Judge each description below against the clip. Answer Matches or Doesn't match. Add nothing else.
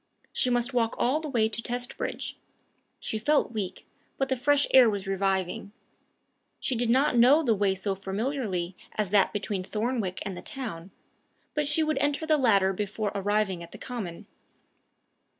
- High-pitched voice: Matches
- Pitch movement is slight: Doesn't match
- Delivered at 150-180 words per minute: Matches